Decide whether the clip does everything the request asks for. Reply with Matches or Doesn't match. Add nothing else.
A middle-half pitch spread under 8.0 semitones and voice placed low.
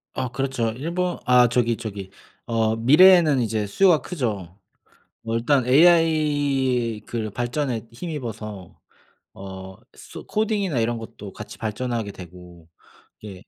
Matches